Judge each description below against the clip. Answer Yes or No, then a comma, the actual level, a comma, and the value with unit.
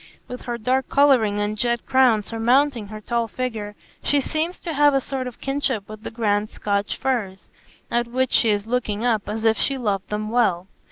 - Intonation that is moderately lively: Yes, average, 3.6 semitones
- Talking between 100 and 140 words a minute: No, average, 200 wpm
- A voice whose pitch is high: Yes, high, 235 Hz